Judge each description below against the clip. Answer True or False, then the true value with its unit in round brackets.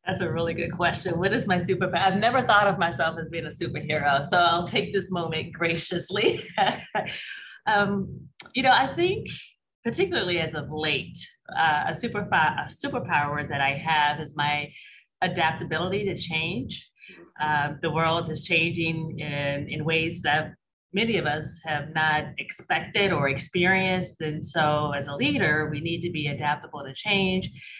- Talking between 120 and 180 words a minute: True (160 wpm)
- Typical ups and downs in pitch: True (3.4 semitones)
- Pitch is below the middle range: False (165 Hz)